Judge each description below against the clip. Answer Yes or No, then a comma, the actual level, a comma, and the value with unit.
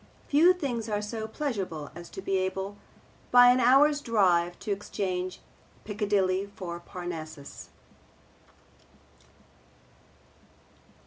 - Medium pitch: No, high, 200 Hz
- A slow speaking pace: Yes, slow, 100 wpm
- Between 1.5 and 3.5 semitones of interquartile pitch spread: No, average, 4.5 semitones